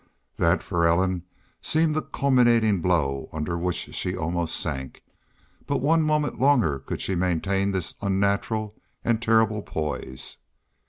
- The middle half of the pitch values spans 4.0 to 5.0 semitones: No, wide, 5.6 semitones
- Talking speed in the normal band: No, slow, 130 wpm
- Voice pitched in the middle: No, very low, 95 Hz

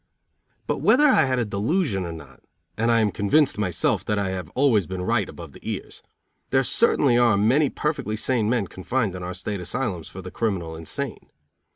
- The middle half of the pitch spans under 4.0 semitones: No, wide, 5.6 semitones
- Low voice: Yes, low, 105 Hz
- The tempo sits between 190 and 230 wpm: Yes, average, 195 wpm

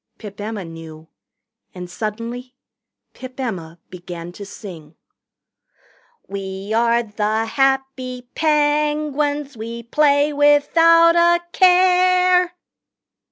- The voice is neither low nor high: No, very high, 250 Hz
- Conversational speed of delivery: No, slow, 90 wpm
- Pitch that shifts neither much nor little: No, wide, 6.7 semitones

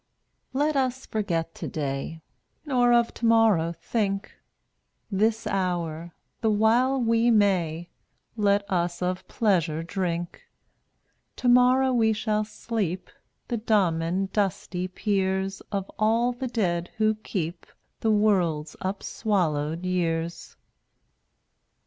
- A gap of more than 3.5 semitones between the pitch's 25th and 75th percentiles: Yes, average, 4.6 semitones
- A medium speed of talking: No, slow, 115 wpm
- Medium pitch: No, high, 195 Hz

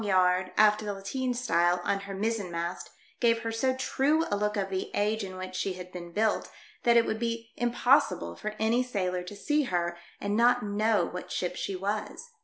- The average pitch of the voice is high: Yes, high, 205 Hz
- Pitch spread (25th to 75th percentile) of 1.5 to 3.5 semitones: No, average, 4.0 semitones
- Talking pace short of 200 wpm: No, fast, 205 wpm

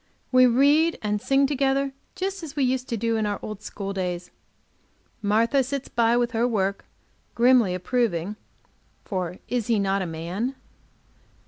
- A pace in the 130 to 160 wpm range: Yes, average, 155 wpm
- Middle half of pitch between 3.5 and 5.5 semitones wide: Yes, average, 5.0 semitones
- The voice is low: No, high, 230 Hz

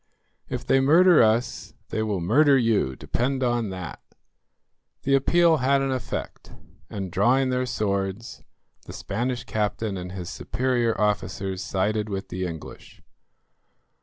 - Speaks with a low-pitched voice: Yes, low, 110 Hz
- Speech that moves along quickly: No, slow, 135 wpm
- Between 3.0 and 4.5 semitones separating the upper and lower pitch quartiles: No, average, 5.1 semitones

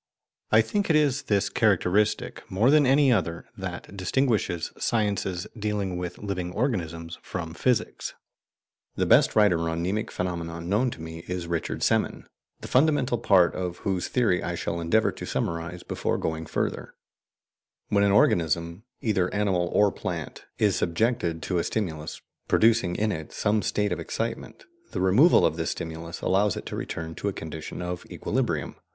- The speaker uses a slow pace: No, average, 160 wpm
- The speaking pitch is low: Yes, very low, 95 Hz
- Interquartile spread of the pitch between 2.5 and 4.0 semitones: No, average, 4.4 semitones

